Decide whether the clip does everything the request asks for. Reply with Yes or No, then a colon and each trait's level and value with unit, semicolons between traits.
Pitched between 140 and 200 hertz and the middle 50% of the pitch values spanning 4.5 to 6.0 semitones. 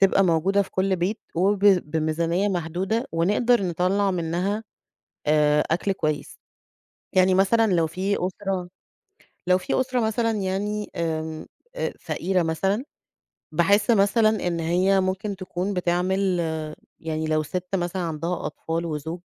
No: medium, 185 Hz; average, 3.1 semitones